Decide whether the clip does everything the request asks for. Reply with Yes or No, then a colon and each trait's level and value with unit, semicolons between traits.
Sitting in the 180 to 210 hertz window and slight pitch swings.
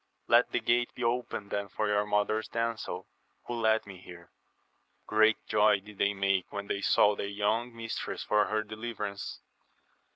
No: low, 105 Hz; narrow, 1.7 semitones